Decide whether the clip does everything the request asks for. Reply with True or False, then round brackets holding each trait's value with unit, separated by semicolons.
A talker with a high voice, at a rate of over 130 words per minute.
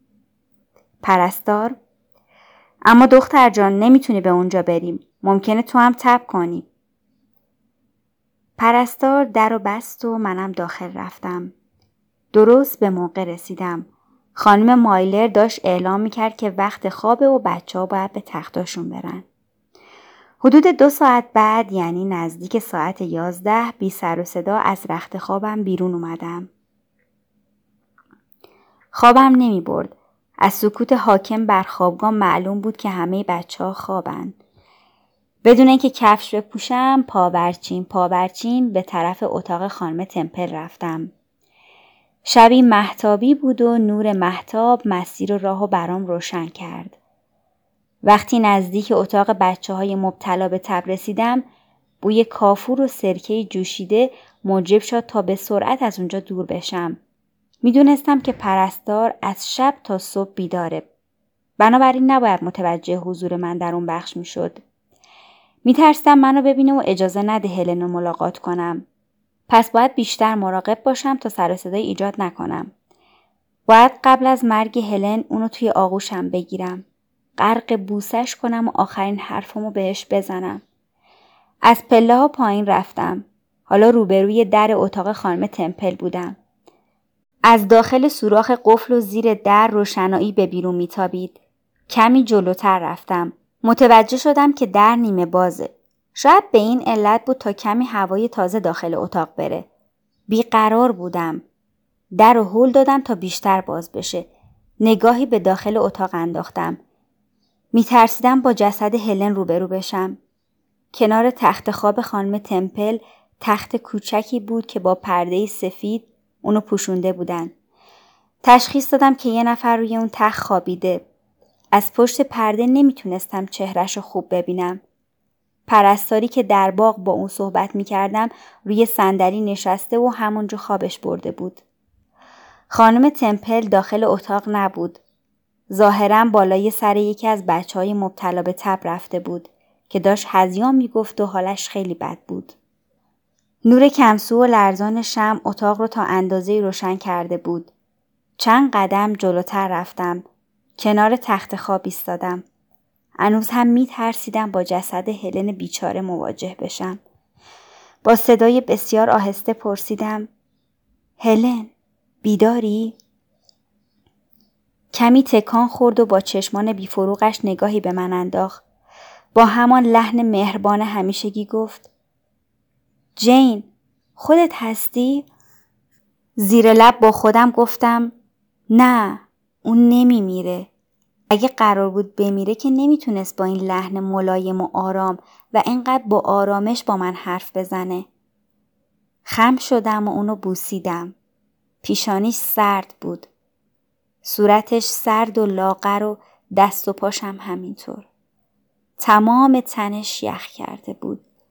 False (210 Hz; 125 wpm)